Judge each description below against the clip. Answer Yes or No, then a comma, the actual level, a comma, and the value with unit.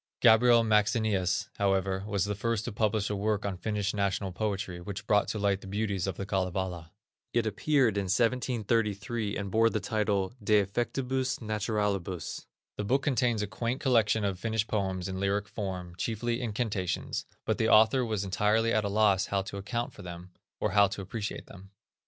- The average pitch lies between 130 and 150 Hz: No, low, 105 Hz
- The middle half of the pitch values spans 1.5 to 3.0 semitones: Yes, narrow, 2.4 semitones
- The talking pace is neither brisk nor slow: Yes, average, 180 wpm